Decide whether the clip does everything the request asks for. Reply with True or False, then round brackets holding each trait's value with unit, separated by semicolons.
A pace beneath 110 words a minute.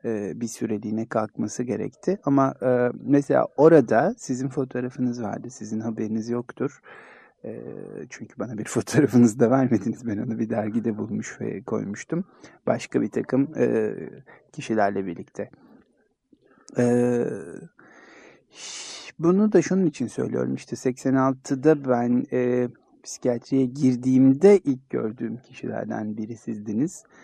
True (100 wpm)